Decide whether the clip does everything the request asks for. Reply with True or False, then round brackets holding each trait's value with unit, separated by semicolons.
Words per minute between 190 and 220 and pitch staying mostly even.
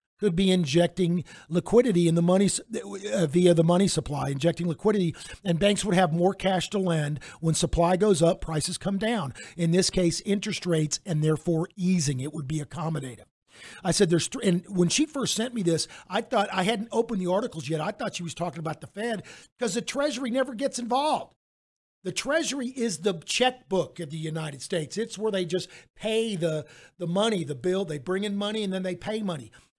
False (205 wpm; 4.1 semitones)